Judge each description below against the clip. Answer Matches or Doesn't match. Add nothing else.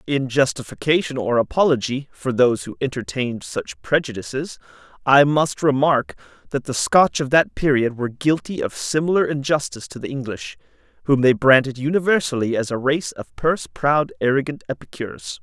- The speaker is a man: Matches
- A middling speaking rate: Matches